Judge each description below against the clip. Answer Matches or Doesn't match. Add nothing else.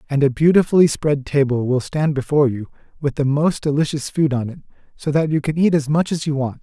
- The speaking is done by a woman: Doesn't match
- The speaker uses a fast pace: Matches